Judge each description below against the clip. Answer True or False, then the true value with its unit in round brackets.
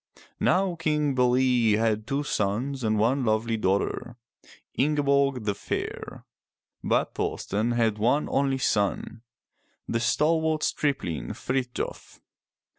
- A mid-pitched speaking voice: False (125 Hz)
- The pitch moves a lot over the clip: False (4.3 semitones)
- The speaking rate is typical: False (115 wpm)